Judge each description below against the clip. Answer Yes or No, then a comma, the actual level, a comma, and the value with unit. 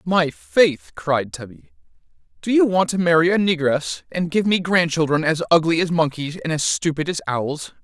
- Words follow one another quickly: No, average, 185 wpm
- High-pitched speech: No, medium, 165 Hz